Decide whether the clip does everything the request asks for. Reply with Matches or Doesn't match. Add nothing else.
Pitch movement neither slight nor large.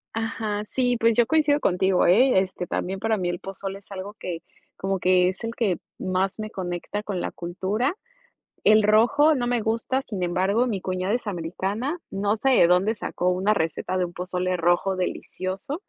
Matches